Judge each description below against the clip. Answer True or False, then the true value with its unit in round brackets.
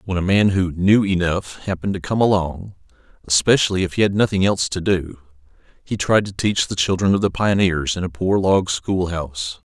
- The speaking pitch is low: True (90 Hz)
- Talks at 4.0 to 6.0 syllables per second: True (5.4 syllables/s)